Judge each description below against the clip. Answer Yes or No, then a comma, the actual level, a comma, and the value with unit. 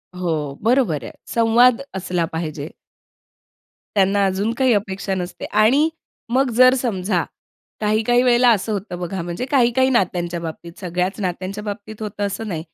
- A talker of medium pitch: No, high, 200 Hz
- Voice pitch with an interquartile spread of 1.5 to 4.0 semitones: No, average, 4.9 semitones